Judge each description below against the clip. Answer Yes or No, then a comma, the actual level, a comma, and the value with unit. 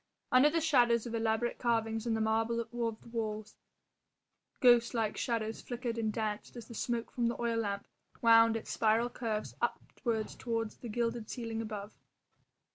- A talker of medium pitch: No, high, 230 Hz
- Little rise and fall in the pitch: Yes, narrow, 1.4 semitones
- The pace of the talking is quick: No, average, 165 wpm